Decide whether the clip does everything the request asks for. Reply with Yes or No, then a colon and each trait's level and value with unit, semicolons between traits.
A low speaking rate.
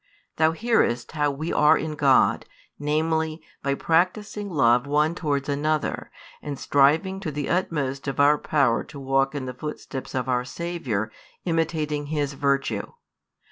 No: average, 145 wpm